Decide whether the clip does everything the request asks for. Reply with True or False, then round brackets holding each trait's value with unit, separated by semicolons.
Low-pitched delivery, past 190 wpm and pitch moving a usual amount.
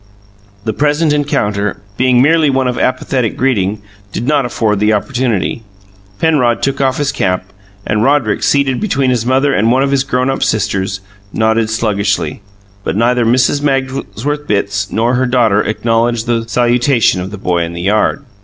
False (120 Hz; 165 wpm; 4.1 semitones)